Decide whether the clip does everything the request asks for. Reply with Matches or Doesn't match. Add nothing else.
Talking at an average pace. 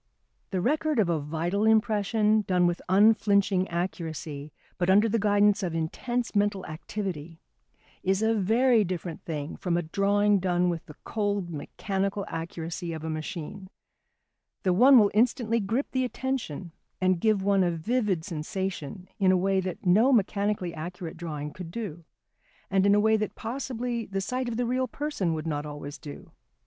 Matches